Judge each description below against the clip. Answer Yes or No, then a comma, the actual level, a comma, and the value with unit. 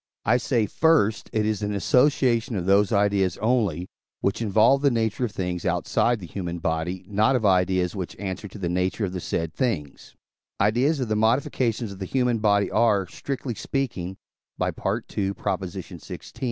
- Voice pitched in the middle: No, low, 105 Hz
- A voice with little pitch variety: No, average, 4.0 semitones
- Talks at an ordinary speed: Yes, average, 165 wpm